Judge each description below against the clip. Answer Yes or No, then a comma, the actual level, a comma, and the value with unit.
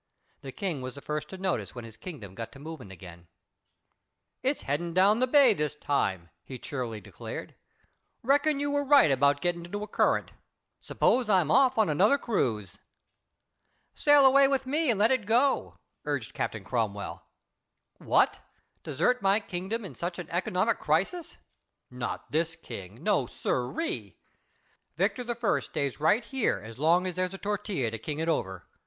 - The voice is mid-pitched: Yes, medium, 175 Hz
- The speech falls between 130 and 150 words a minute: No, average, 165 wpm